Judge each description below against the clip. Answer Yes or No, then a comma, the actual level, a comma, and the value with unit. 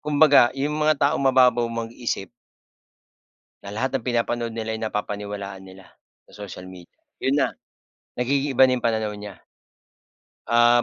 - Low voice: Yes, low, 120 Hz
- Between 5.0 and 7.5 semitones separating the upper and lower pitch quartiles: No, average, 4.3 semitones